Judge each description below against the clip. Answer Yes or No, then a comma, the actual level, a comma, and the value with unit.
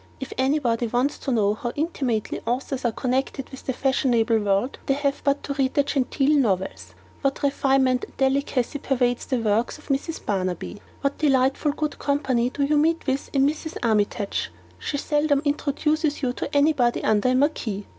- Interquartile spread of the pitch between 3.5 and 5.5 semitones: No, average, 3.0 semitones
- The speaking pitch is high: Yes, very high, 270 Hz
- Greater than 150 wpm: Yes, average, 175 wpm